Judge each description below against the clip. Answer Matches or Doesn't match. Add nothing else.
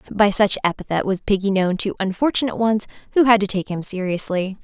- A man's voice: Doesn't match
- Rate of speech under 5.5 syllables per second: Doesn't match